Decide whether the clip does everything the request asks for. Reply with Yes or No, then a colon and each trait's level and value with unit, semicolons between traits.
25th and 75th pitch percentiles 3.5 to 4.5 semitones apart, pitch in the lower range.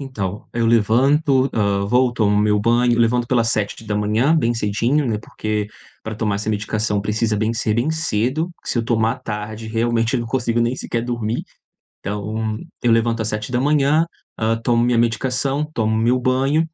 No: narrow, 2.6 semitones; low, 115 Hz